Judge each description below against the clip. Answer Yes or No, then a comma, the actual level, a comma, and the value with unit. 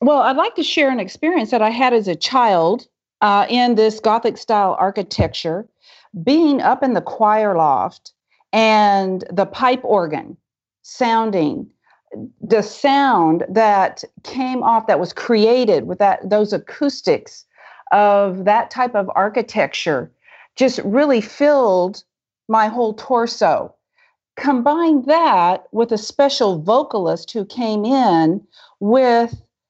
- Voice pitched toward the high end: Yes, high, 225 Hz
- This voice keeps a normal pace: No, slow, 125 wpm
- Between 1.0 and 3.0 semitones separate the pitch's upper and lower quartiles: No, average, 4.4 semitones